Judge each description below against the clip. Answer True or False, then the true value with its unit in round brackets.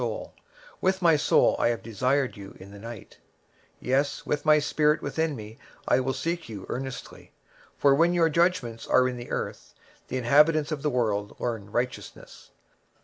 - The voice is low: True (130 Hz)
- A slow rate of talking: False (175 wpm)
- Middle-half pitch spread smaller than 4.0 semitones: False (4.8 semitones)